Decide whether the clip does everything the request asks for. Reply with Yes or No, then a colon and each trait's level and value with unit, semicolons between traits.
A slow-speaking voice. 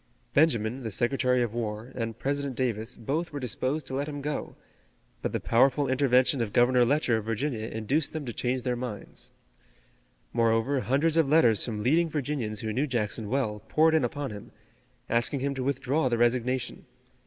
No: average, 175 wpm